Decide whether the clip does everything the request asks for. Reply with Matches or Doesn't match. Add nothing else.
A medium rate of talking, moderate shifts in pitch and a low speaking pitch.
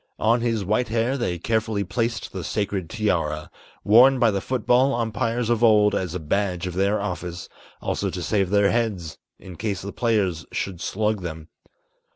Matches